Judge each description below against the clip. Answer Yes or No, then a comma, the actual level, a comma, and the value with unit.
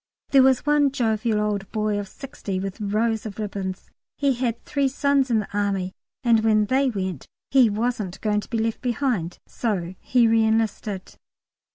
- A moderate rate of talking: Yes, average, 175 wpm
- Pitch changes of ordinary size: Yes, average, 3.6 semitones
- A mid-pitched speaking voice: No, high, 220 Hz